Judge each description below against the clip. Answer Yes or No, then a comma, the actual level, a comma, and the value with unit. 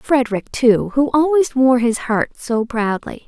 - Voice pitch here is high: Yes, very high, 250 Hz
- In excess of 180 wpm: No, average, 165 wpm